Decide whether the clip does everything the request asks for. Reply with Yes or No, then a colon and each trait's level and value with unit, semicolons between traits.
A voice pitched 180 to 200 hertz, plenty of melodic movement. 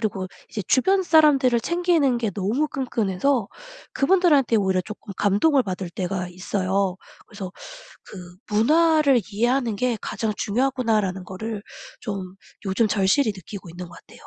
No: high, 215 Hz; wide, 5.9 semitones